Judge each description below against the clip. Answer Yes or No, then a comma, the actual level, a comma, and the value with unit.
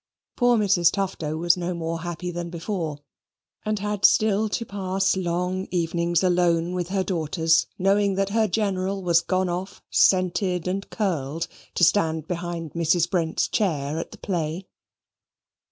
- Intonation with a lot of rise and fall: No, narrow, 2.6 semitones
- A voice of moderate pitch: Yes, medium, 180 Hz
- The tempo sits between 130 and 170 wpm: Yes, average, 150 wpm